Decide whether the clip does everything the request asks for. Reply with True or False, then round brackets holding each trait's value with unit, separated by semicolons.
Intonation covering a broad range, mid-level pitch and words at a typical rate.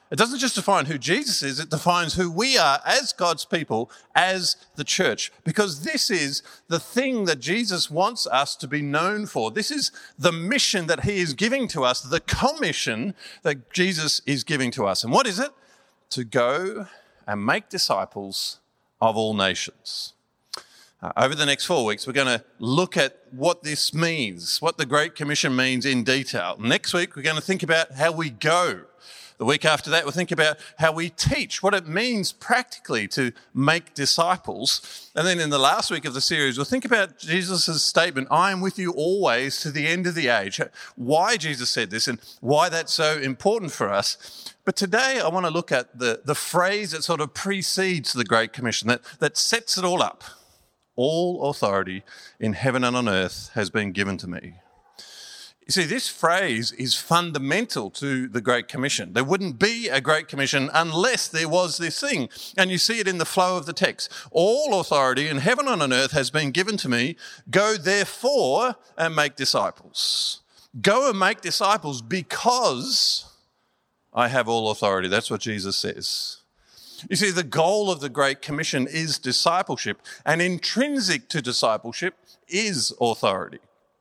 True (5.8 semitones; 160 Hz; 185 wpm)